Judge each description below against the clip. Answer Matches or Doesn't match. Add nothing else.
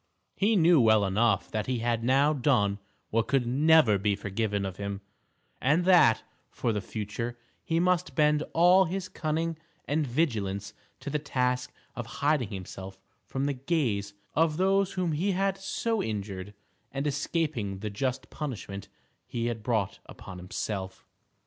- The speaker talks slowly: Doesn't match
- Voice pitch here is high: Doesn't match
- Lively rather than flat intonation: Matches